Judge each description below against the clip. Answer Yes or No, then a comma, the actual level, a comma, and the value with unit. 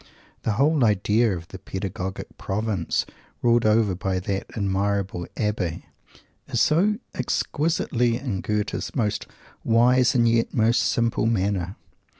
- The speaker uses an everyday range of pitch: Yes, average, 3.5 semitones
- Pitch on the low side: Yes, low, 105 Hz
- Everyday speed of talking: No, slow, 125 wpm